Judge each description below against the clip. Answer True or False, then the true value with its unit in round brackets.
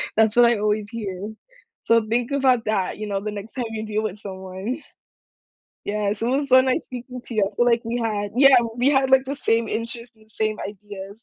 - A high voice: True (225 Hz)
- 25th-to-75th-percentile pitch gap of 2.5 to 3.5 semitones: True (2.9 semitones)